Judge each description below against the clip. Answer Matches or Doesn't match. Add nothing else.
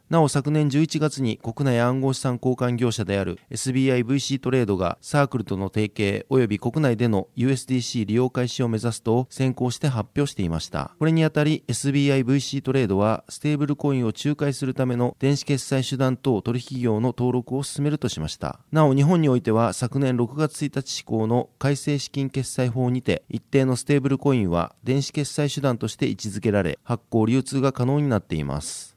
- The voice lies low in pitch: Matches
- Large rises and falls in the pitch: Doesn't match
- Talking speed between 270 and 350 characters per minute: Doesn't match